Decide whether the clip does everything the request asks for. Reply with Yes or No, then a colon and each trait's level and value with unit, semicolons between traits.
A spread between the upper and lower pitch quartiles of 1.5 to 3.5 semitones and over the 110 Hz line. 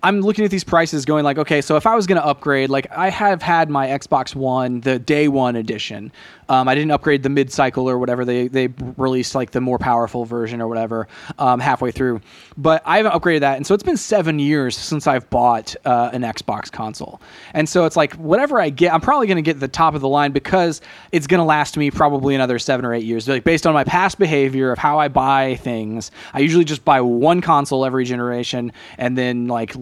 No: average, 4.4 semitones; medium, 140 Hz